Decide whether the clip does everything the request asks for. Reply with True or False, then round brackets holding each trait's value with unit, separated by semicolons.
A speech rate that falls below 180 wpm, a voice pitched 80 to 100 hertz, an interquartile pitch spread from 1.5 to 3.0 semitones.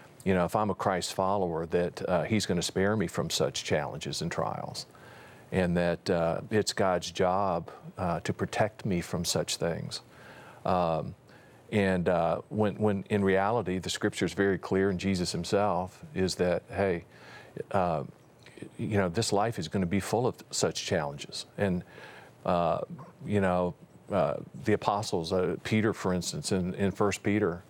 True (170 wpm; 95 Hz; 2.5 semitones)